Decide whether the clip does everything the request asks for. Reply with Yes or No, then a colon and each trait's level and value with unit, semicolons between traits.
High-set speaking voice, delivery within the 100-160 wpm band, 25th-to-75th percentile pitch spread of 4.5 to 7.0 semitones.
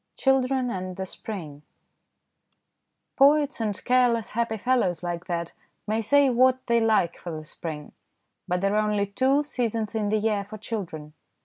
Yes: high, 215 Hz; average, 155 wpm; average, 5.3 semitones